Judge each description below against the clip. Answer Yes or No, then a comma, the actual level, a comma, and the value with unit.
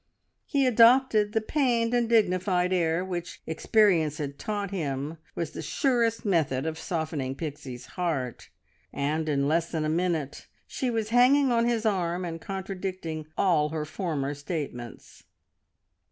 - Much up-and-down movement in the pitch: Yes, wide, 6.0 semitones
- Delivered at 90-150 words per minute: Yes, average, 140 wpm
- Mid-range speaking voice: Yes, medium, 175 Hz